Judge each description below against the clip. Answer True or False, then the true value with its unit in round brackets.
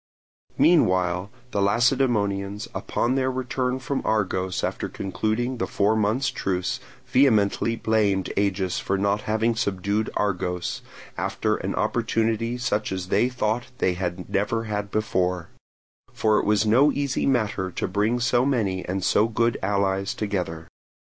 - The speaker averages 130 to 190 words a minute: True (140 wpm)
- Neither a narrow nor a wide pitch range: True (3.6 semitones)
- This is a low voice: True (105 Hz)